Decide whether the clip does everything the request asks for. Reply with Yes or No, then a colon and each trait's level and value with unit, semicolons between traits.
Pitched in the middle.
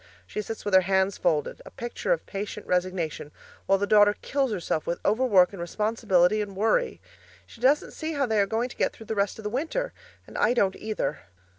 No: high, 210 Hz